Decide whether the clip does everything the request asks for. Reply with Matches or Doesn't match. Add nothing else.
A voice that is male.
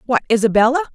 Doesn't match